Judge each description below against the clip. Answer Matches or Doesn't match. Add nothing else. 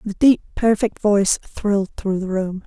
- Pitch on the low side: Doesn't match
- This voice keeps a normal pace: Matches